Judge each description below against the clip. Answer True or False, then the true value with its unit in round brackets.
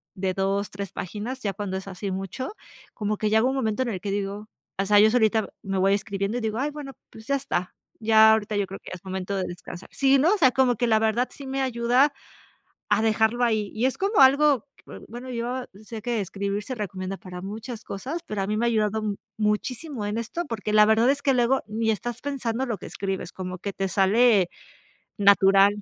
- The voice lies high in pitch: True (220 Hz)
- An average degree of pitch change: True (3.7 semitones)